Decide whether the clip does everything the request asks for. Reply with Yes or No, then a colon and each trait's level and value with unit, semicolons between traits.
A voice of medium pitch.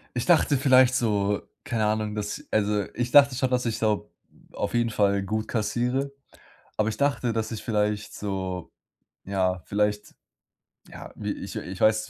No: low, 110 Hz